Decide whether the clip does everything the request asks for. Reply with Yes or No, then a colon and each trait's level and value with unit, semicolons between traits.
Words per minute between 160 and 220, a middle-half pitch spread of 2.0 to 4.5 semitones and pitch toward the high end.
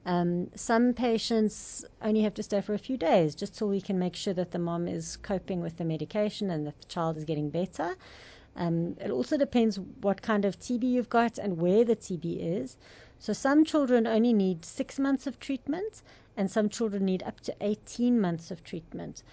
No: fast, 205 wpm; average, 4.9 semitones; high, 205 Hz